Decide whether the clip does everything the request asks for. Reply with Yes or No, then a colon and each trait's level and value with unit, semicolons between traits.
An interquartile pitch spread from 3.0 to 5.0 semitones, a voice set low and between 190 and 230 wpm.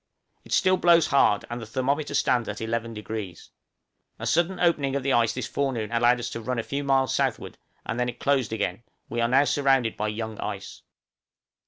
Yes: average, 3.6 semitones; low, 125 Hz; average, 195 wpm